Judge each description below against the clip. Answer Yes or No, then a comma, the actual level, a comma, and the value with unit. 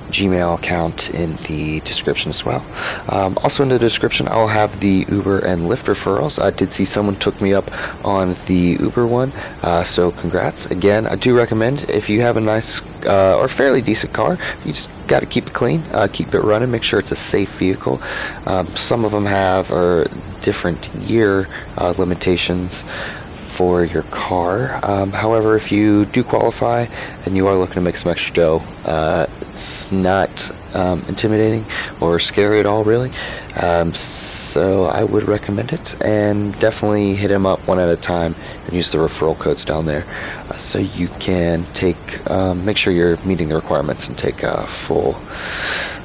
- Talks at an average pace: Yes, average, 185 wpm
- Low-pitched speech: Yes, very low, 95 Hz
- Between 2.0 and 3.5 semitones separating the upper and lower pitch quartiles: Yes, average, 3.1 semitones